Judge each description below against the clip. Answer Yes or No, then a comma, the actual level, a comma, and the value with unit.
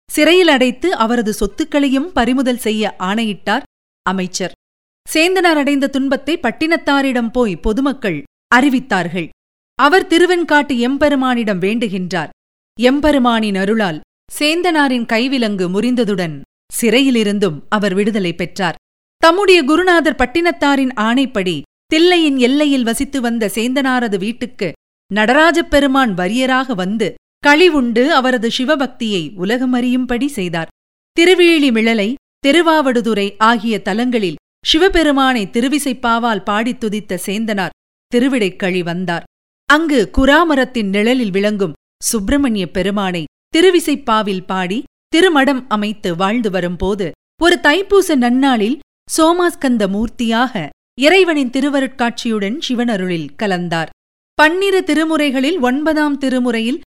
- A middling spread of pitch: No, wide, 5.7 semitones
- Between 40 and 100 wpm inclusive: Yes, average, 85 wpm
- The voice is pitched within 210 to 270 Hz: Yes, high, 245 Hz